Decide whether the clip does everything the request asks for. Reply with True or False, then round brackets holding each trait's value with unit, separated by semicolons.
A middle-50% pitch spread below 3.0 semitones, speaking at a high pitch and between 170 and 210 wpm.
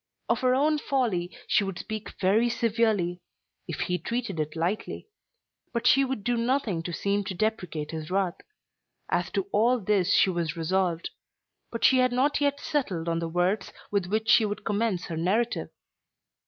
False (5.1 semitones; 205 Hz; 175 wpm)